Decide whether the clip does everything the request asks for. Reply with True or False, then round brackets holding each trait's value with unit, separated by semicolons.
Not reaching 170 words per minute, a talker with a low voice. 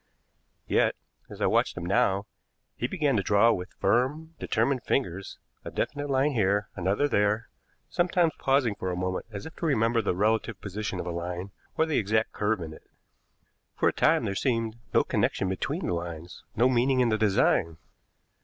False (180 wpm; 110 Hz)